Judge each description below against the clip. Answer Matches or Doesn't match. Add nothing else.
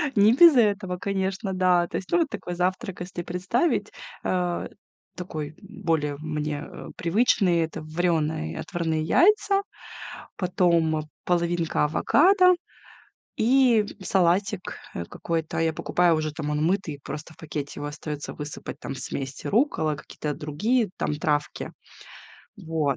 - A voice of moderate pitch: Matches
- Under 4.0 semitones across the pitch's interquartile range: Doesn't match